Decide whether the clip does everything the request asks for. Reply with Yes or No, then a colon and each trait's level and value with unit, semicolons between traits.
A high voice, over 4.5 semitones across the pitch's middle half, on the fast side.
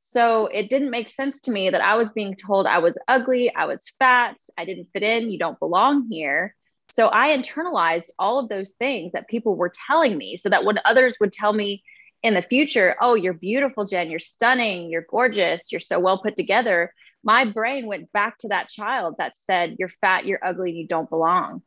Yes: high, 210 Hz; average, 5.1 semitones; fast, 215 wpm